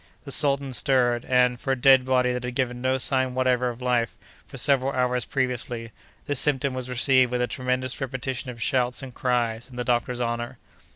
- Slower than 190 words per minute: No, average, 195 wpm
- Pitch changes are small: Yes, narrow, 1.2 semitones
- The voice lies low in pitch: Yes, low, 125 Hz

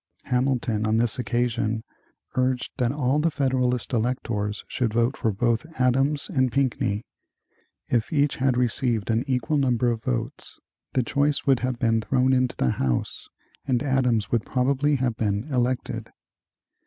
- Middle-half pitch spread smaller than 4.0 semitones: Yes, narrow, 2.4 semitones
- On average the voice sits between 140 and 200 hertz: No, low, 125 Hz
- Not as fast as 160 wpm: Yes, average, 150 wpm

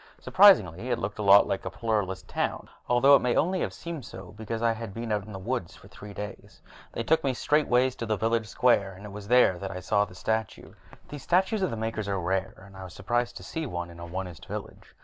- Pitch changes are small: No, average, 4.2 semitones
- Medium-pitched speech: No, low, 110 Hz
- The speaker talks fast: Yes, fast, 245 wpm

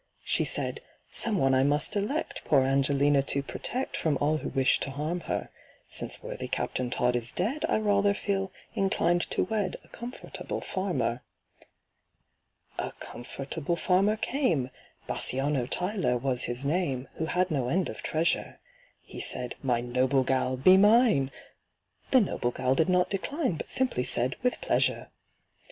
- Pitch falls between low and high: Yes, medium, 155 Hz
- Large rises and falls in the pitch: Yes, wide, 6.8 semitones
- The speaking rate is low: No, average, 155 wpm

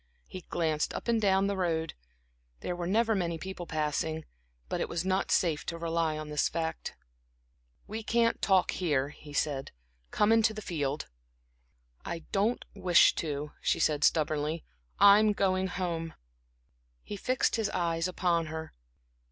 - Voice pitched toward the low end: No, medium, 170 Hz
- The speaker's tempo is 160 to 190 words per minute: No, average, 150 wpm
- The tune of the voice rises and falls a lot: No, average, 3.7 semitones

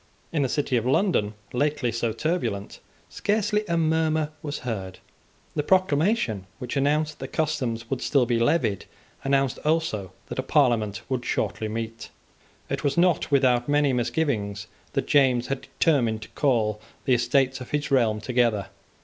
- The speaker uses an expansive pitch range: No, average, 4.8 semitones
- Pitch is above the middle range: No, low, 130 Hz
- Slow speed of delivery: No, average, 160 wpm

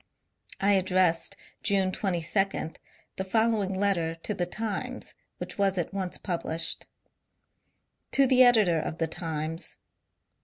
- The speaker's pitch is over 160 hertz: Yes, high, 190 Hz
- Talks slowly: Yes, slow, 130 wpm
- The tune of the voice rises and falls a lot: No, average, 3.2 semitones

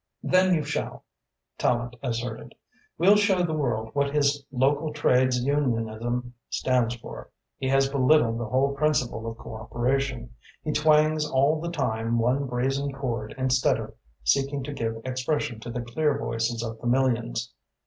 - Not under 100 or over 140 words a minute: No, average, 150 wpm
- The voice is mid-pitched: No, low, 130 Hz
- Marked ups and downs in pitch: No, average, 3.4 semitones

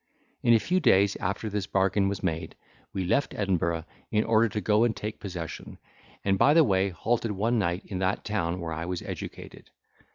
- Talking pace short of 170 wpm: No, average, 195 wpm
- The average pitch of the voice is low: Yes, low, 100 Hz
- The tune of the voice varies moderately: Yes, average, 3.2 semitones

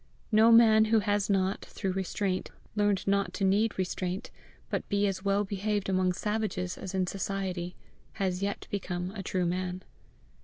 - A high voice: Yes, high, 195 Hz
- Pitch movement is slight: Yes, narrow, 1.8 semitones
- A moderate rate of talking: Yes, average, 160 wpm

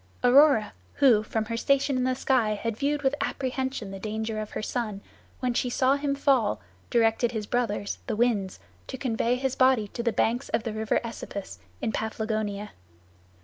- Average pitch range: Yes, average, 3.2 semitones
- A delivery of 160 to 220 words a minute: Yes, average, 180 wpm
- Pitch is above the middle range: Yes, high, 230 Hz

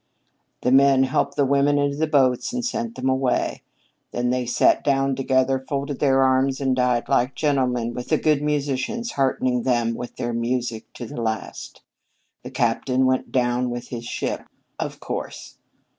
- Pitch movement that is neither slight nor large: No, narrow, 2.2 semitones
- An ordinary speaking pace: Yes, average, 170 wpm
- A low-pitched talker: Yes, low, 130 Hz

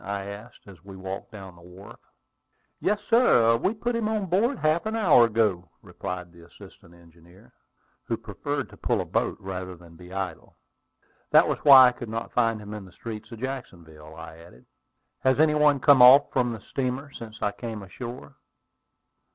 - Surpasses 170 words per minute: Yes, average, 185 wpm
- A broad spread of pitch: Yes, wide, 6.6 semitones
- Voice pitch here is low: Yes, low, 110 Hz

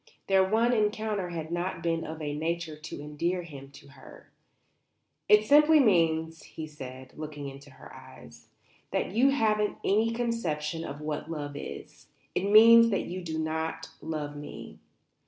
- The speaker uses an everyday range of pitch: No, wide, 5.7 semitones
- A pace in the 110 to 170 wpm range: Yes, average, 155 wpm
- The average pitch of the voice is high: No, medium, 165 Hz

